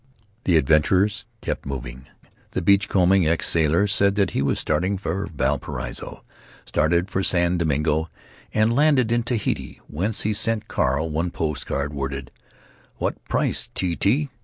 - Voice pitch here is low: Yes, very low, 85 Hz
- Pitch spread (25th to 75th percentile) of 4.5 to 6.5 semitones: Yes, average, 5.1 semitones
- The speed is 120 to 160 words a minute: Yes, average, 150 wpm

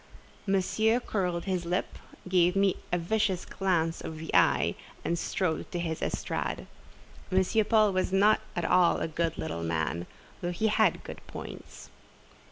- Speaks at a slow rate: No, average, 155 wpm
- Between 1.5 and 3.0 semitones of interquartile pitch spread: Yes, average, 2.7 semitones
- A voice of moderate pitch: Yes, medium, 180 Hz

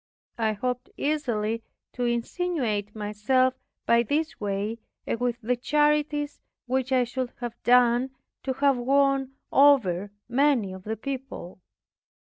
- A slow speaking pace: Yes, slow, 125 wpm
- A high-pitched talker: Yes, high, 245 Hz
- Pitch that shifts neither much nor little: Yes, average, 3.7 semitones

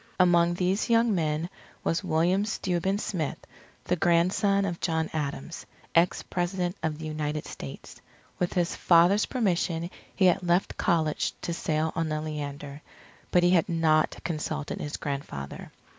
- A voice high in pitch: No, medium, 170 Hz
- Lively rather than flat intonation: No, average, 2.7 semitones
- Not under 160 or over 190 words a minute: No, average, 145 wpm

